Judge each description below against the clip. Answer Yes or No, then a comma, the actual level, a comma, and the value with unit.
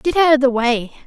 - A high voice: Yes, very high, 270 Hz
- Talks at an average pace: No, fast, 280 wpm